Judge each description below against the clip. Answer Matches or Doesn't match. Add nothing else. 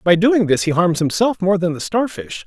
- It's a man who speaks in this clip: Matches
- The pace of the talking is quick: Matches